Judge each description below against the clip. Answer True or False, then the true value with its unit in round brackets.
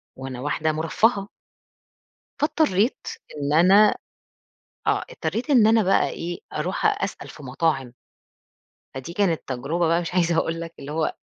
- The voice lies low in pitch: False (170 Hz)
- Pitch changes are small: False (4.8 semitones)